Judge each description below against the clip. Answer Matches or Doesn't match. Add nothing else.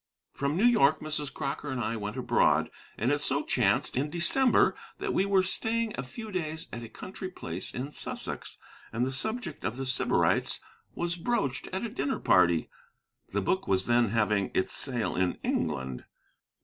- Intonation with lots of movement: Matches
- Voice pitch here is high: Doesn't match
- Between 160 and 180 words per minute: Matches